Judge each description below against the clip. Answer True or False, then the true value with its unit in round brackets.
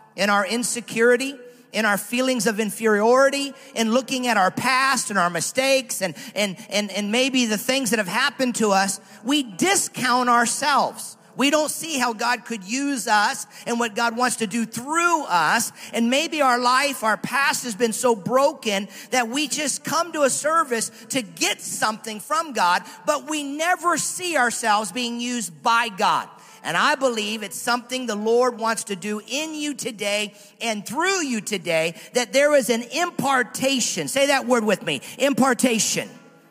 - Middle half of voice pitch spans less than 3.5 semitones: False (3.8 semitones)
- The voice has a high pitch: True (240 Hz)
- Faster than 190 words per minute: False (175 wpm)